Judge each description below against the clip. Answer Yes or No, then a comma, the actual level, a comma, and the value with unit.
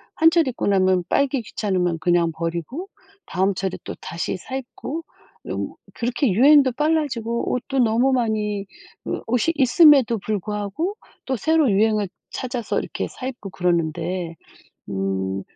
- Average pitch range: No, wide, 6.3 semitones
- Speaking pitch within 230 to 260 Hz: No, high, 220 Hz